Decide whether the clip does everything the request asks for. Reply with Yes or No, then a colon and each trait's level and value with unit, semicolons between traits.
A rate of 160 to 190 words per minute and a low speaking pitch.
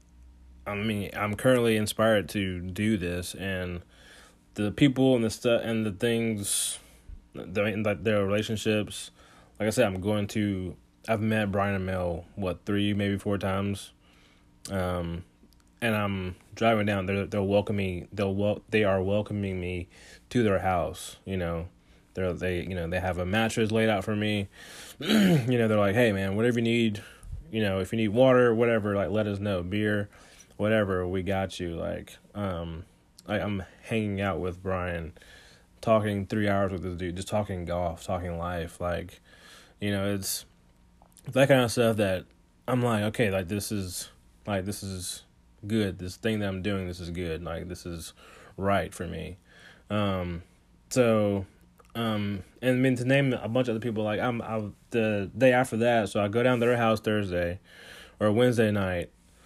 Yes: average, 180 wpm; low, 100 Hz